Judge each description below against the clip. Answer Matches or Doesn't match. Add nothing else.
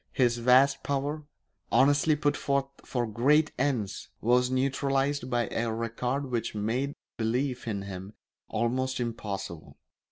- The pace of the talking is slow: Matches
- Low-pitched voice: Matches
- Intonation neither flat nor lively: Matches